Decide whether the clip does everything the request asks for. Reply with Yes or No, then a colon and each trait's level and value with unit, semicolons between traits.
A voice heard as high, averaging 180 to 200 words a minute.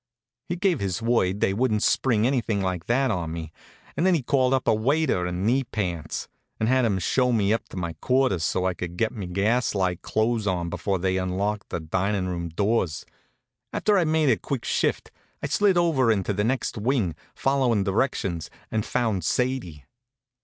No: low, 105 Hz; average, 190 wpm